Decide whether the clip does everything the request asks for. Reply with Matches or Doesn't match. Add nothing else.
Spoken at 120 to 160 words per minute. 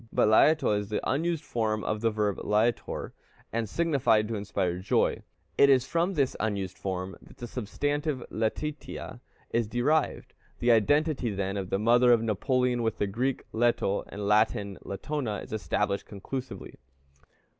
Matches